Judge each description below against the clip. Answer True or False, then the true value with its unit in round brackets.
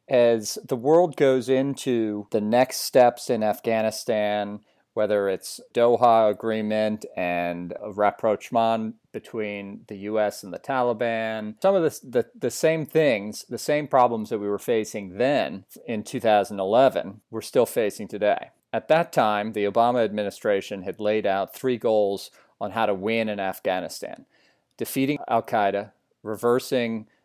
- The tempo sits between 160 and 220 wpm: False (145 wpm)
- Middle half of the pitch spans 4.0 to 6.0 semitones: False (3.0 semitones)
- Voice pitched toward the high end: False (110 Hz)